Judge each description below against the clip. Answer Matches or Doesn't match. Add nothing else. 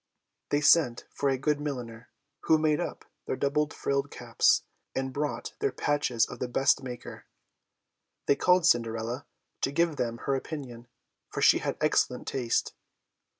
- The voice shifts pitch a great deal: Doesn't match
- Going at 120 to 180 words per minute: Matches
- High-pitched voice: Doesn't match